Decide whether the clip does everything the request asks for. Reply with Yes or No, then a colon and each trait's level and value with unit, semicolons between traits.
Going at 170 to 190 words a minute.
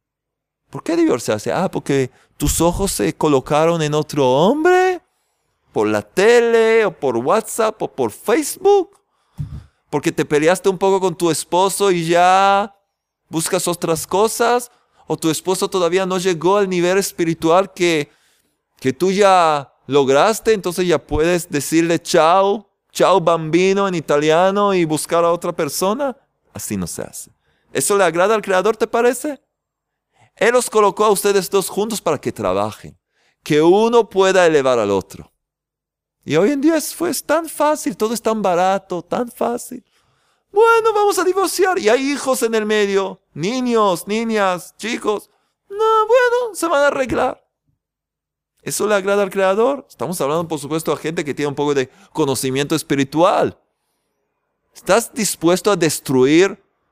No: average, 150 wpm